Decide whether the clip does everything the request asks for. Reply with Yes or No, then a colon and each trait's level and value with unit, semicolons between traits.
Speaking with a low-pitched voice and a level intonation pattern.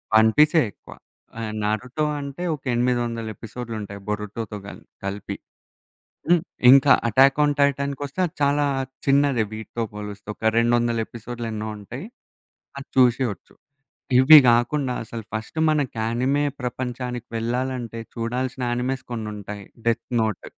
No: low, 120 Hz; average, 3.5 semitones